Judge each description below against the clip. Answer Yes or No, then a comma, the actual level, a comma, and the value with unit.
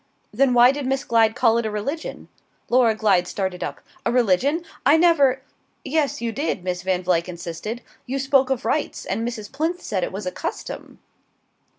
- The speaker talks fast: No, average, 190 wpm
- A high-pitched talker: Yes, high, 235 Hz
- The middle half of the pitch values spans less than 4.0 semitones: No, wide, 5.6 semitones